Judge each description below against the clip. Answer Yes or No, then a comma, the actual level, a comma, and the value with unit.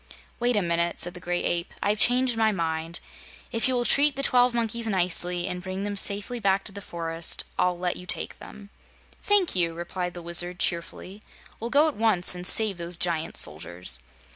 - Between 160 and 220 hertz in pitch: Yes, medium, 185 Hz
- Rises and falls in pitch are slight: No, average, 4.6 semitones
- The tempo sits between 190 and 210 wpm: Yes, average, 195 wpm